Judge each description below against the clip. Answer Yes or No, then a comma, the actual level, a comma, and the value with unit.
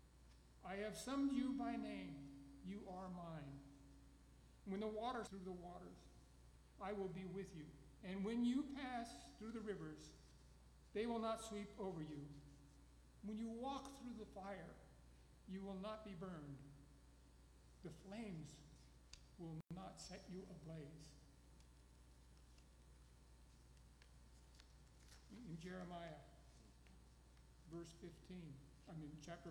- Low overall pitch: No, medium, 150 Hz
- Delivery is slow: Yes, slow, 120 wpm